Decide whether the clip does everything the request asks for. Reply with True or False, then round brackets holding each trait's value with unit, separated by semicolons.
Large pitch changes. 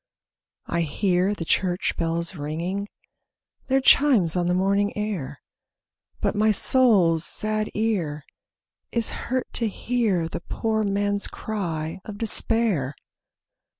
False (4.4 semitones)